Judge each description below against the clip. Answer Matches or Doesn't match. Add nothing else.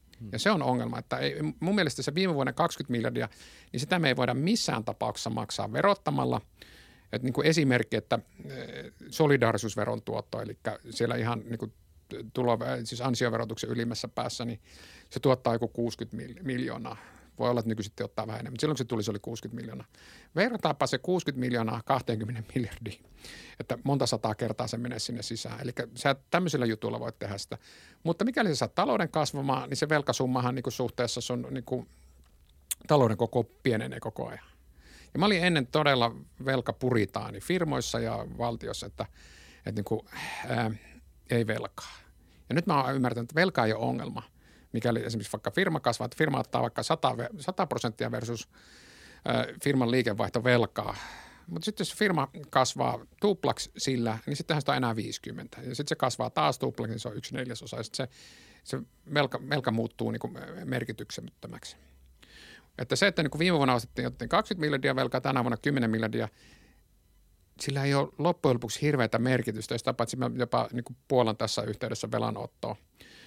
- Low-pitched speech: Matches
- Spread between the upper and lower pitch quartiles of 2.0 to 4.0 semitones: Matches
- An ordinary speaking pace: Doesn't match